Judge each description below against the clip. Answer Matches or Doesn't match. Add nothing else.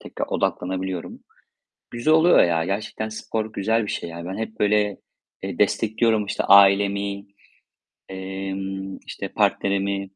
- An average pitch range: Doesn't match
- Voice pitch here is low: Matches